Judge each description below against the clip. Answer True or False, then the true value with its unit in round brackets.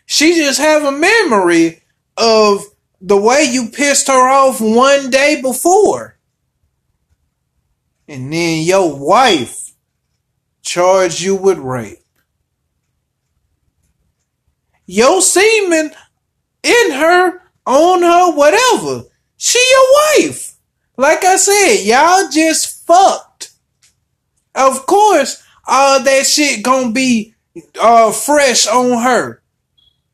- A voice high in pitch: True (270 Hz)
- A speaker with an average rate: False (100 wpm)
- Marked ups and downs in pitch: True (7.8 semitones)